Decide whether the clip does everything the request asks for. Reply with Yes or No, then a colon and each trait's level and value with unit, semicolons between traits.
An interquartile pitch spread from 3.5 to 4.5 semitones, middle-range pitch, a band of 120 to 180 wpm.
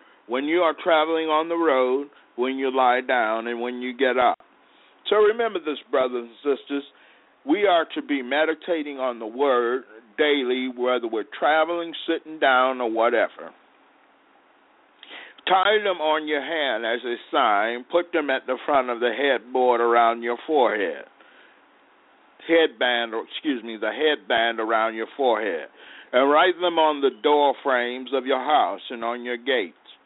No: average, 4.2 semitones; low, 130 Hz; average, 160 wpm